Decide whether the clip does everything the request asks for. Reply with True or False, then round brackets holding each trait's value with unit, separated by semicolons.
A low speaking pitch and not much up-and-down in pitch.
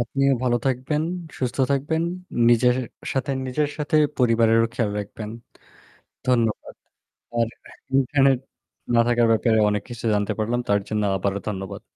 False (120 Hz; 3.4 semitones)